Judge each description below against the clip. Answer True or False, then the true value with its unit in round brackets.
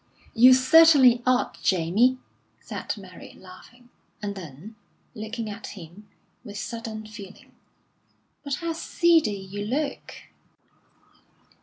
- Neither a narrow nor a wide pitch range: True (4.2 semitones)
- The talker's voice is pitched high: True (220 Hz)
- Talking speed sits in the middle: False (105 wpm)